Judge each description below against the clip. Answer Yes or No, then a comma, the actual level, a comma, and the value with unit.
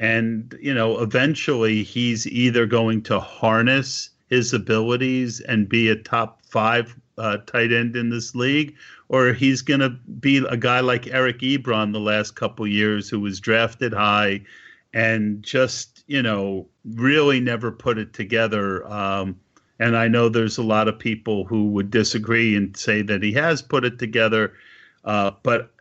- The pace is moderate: Yes, average, 165 wpm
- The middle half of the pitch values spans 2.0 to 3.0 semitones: Yes, average, 2.7 semitones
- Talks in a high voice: No, low, 115 Hz